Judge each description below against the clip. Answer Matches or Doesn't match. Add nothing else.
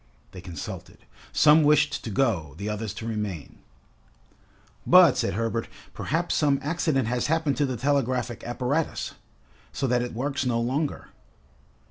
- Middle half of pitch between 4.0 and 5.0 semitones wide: Matches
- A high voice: Doesn't match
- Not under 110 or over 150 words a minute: Matches